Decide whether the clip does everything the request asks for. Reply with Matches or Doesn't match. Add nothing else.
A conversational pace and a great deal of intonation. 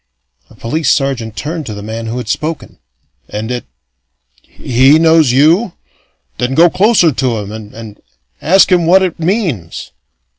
Matches